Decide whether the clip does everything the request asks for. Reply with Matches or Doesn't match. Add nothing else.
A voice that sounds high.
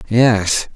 Doesn't match